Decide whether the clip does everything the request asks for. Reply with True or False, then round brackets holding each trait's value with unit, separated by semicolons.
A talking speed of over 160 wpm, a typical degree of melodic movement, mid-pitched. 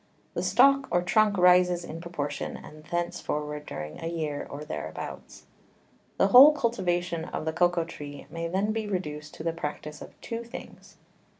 True (170 wpm; 4.1 semitones; 170 Hz)